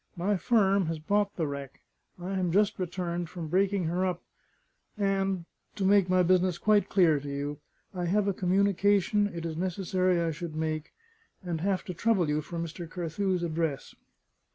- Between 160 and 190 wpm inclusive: Yes, average, 175 wpm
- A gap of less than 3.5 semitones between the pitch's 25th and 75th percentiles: Yes, average, 2.9 semitones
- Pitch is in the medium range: Yes, medium, 180 Hz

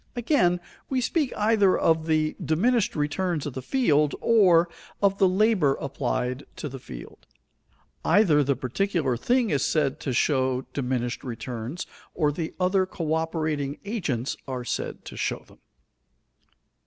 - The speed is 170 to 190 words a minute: No, average, 140 wpm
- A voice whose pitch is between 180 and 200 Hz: No, medium, 155 Hz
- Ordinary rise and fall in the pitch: No, wide, 6.2 semitones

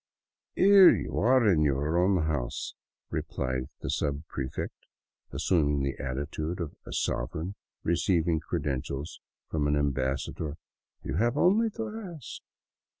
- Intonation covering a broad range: Yes, wide, 6.0 semitones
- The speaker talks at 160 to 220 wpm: No, average, 140 wpm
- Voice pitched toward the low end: Yes, very low, 80 Hz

